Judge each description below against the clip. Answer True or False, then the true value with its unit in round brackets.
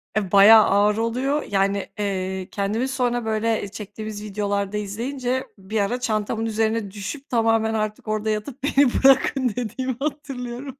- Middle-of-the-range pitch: False (220 Hz)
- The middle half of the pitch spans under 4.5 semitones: True (3.4 semitones)